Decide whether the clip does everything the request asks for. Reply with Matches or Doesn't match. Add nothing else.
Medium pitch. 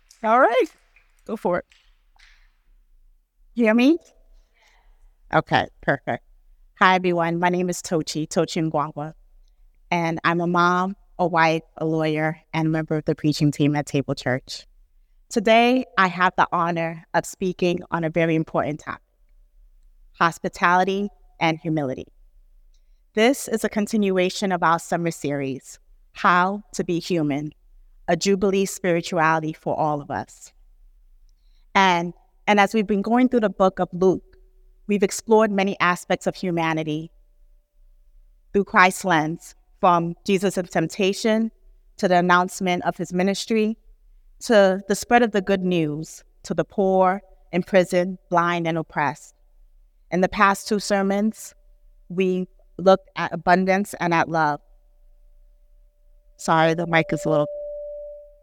Matches